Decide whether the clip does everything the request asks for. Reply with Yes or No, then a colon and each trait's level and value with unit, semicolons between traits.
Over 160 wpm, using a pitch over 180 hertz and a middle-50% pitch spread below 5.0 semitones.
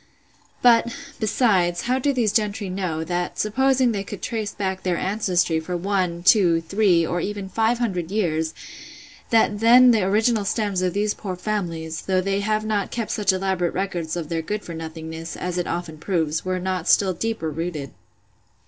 Yes: average, 175 wpm; high, 190 Hz; average, 3.7 semitones